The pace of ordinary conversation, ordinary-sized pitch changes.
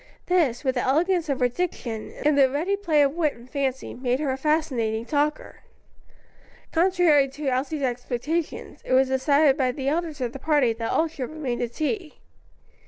Yes: average, 180 wpm; average, 3.5 semitones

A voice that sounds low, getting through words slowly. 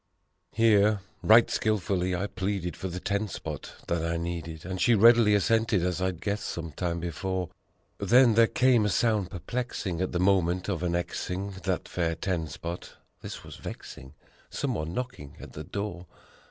No: very low, 95 Hz; average, 165 wpm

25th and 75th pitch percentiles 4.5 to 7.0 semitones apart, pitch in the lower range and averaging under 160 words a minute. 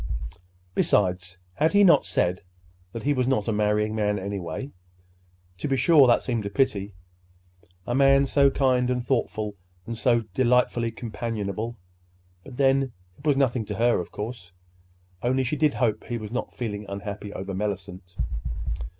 Yes: average, 4.9 semitones; low, 110 Hz; average, 150 wpm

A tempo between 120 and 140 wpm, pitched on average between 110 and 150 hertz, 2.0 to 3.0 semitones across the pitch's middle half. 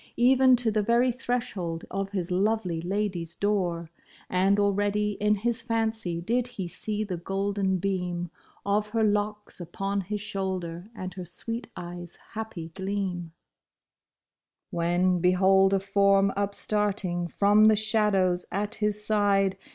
No: slow, 135 wpm; high, 200 Hz; narrow, 2.6 semitones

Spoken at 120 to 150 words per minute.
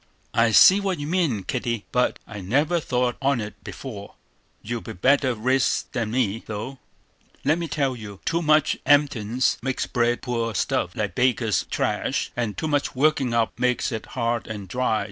No: average, 170 wpm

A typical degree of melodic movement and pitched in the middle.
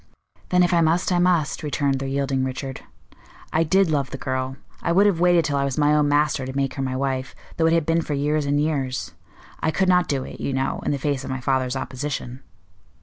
Yes: average, 3.5 semitones; medium, 145 Hz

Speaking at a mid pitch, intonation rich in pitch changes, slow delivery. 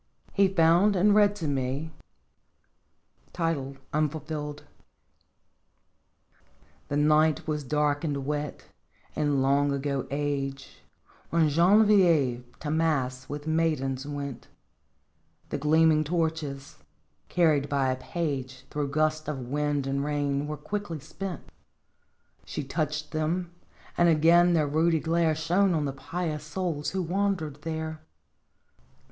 No: medium, 150 Hz; average, 2.7 semitones; slow, 115 wpm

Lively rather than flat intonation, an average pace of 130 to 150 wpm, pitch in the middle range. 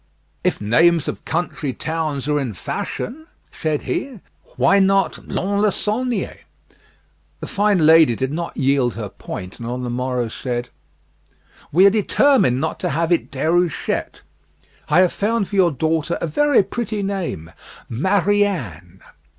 Yes: wide, 7.5 semitones; average, 140 wpm; medium, 165 Hz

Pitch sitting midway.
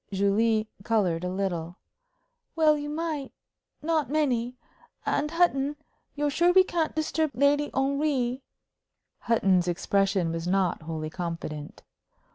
No: high, 240 Hz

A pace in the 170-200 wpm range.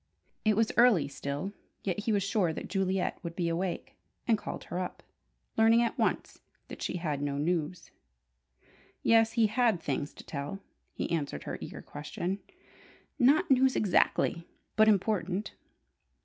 No: average, 150 wpm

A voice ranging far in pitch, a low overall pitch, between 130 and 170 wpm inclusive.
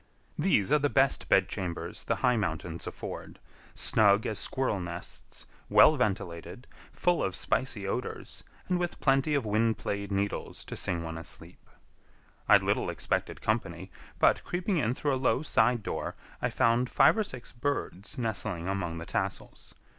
Yes: wide, 6.1 semitones; low, 110 Hz; average, 155 wpm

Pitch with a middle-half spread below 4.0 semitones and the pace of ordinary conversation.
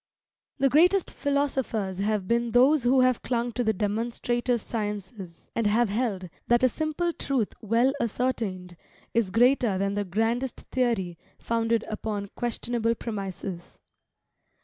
No: average, 3.4 semitones; slow, 130 wpm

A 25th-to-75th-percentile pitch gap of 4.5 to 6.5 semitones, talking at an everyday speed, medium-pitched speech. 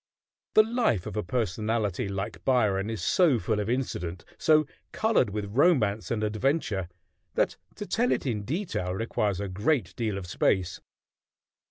No: wide, 5.4 semitones; average, 155 wpm; low, 110 Hz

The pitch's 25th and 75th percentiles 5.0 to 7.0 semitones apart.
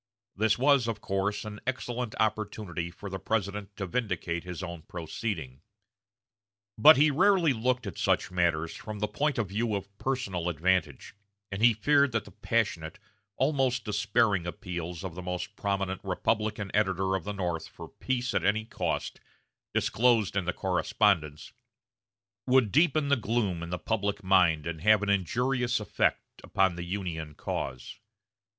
No: average, 4.5 semitones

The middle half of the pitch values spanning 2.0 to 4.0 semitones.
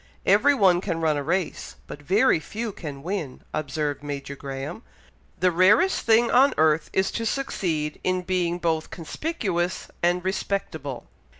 No: average, 4.6 semitones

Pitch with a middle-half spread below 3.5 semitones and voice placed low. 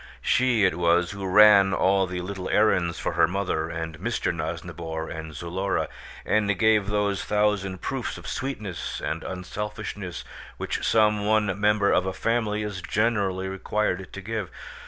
Yes: narrow, 2.6 semitones; low, 100 Hz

